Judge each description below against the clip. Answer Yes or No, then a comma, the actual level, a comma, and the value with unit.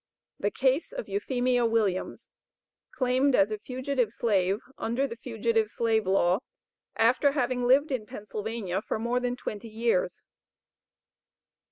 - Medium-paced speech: No, slow, 130 wpm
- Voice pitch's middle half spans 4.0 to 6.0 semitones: No, average, 3.1 semitones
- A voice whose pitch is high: Yes, high, 235 Hz